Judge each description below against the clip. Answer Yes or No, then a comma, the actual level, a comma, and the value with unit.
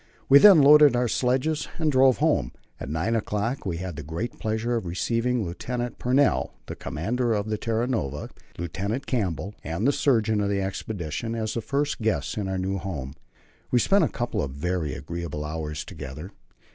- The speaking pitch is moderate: No, low, 105 Hz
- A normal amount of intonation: No, wide, 6.7 semitones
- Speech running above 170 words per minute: Yes, average, 185 wpm